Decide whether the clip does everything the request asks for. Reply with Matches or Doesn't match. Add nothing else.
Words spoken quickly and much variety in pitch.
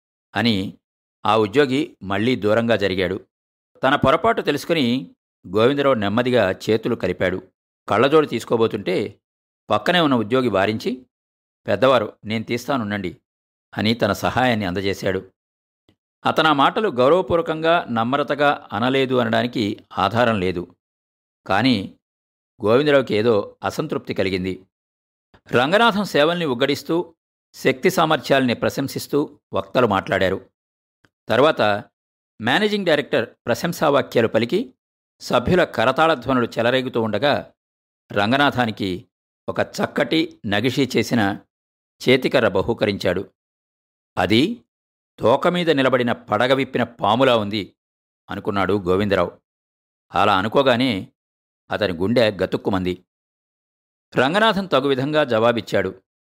Doesn't match